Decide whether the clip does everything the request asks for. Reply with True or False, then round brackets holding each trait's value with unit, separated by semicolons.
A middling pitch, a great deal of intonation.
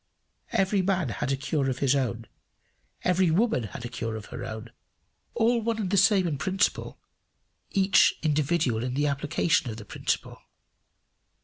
True (150 Hz; 7.3 semitones)